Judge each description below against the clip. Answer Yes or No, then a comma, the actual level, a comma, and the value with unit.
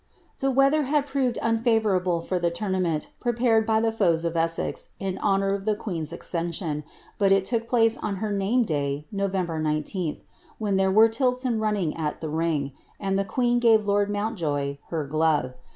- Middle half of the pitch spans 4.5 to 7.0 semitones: Yes, average, 5.2 semitones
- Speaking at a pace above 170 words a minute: Yes, average, 180 wpm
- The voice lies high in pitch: Yes, high, 195 Hz